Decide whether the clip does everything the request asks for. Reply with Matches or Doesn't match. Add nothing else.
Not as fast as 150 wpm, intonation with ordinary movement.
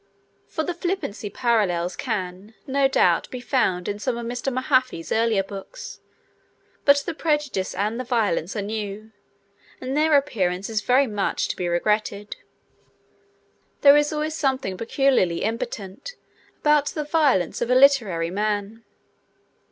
Doesn't match